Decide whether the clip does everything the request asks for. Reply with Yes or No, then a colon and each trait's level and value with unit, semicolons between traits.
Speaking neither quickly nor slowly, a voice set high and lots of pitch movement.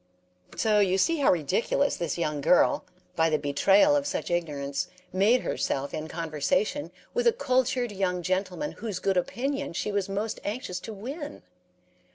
Yes: average, 165 wpm; high, 195 Hz; wide, 7.1 semitones